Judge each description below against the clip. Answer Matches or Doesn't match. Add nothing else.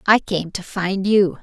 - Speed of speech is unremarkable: Doesn't match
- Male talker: Doesn't match